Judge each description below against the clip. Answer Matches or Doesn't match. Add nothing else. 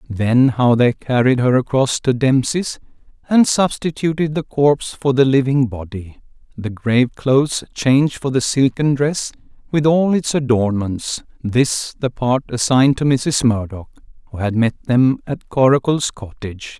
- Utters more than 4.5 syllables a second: Doesn't match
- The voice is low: Matches